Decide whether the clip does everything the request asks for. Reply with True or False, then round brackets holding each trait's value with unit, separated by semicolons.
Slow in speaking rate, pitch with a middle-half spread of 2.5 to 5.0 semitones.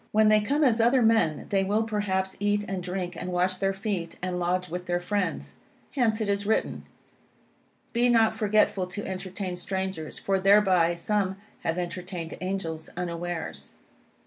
False (160 wpm; 2.8 semitones)